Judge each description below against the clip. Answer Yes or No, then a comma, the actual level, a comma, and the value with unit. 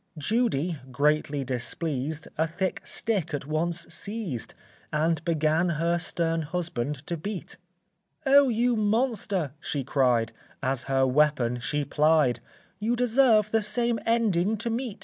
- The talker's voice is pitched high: No, medium, 165 Hz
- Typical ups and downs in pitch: No, wide, 6.7 semitones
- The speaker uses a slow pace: Yes, slow, 130 wpm